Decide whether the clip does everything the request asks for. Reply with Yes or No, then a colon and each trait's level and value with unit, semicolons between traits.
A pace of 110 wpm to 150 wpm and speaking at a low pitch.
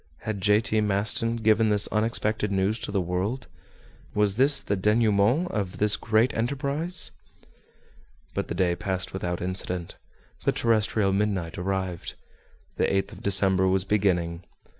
Yes: average, 140 wpm; low, 100 Hz